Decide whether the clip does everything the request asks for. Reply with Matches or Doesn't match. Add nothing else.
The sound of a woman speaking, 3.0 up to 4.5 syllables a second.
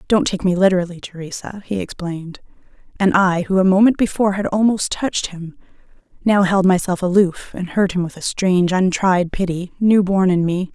Doesn't match